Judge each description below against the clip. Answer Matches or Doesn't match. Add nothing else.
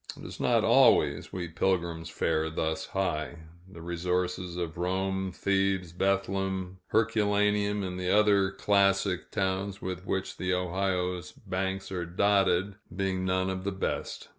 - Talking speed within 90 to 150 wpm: Matches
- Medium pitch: Doesn't match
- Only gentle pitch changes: Matches